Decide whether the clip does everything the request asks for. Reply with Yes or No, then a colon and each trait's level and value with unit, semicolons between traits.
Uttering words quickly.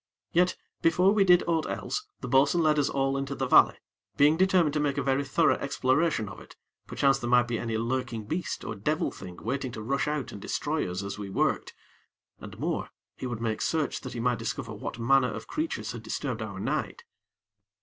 Yes: fast, 210 wpm